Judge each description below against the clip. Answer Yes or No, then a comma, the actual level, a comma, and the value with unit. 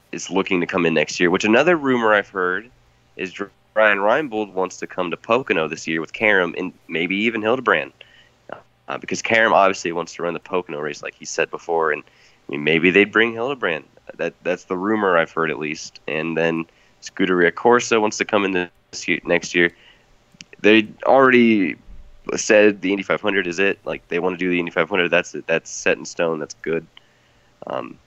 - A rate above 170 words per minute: Yes, average, 200 wpm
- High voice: No, very low, 95 Hz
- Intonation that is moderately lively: Yes, average, 4.3 semitones